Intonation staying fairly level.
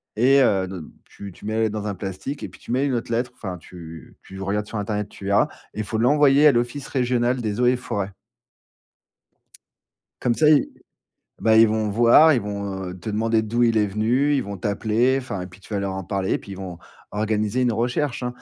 No: average, 3.7 semitones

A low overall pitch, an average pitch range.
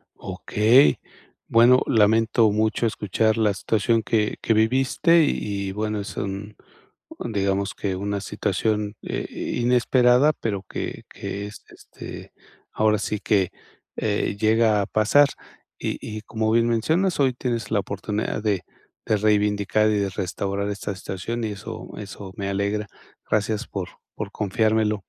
No: low, 105 Hz; narrow, 2.0 semitones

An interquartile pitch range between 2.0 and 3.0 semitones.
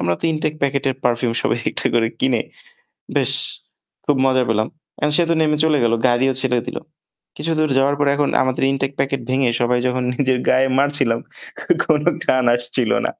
Yes: average, 2.7 semitones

